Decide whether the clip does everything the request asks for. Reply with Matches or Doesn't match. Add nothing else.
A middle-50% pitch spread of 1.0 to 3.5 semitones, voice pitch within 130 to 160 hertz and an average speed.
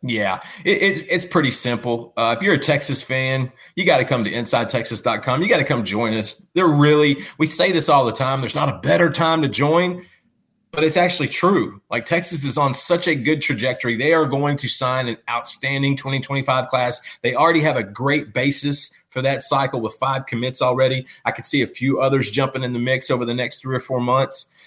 Doesn't match